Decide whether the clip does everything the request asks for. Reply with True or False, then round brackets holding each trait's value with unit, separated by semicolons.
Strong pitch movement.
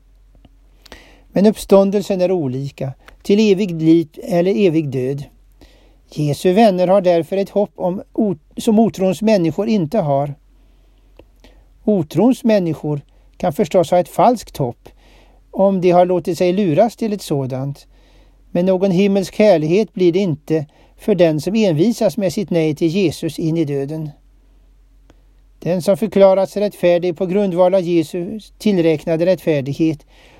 False (4.0 semitones)